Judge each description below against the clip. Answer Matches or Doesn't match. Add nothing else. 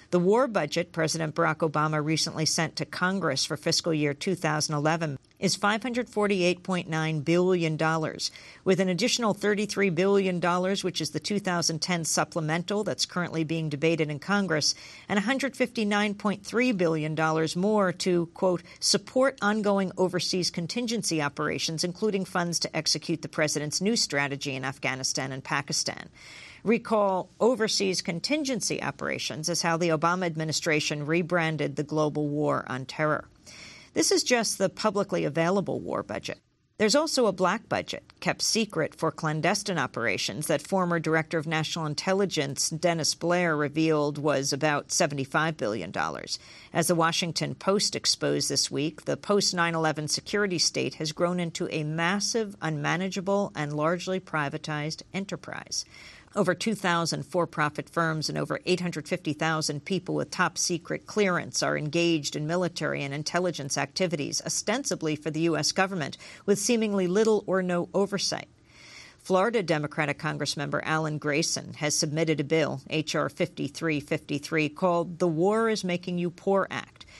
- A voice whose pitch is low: Doesn't match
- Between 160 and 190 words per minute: Doesn't match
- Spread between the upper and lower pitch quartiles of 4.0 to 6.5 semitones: Doesn't match